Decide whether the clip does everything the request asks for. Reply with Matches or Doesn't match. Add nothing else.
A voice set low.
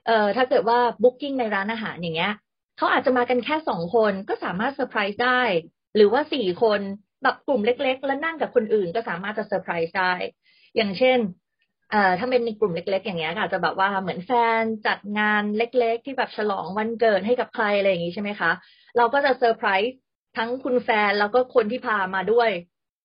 Doesn't match